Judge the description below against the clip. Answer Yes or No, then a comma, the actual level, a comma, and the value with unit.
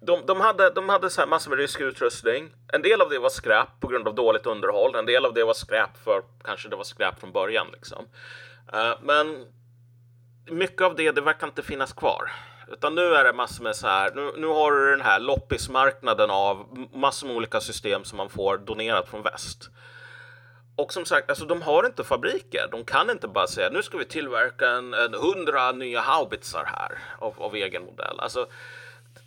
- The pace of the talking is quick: Yes, fast, 205 wpm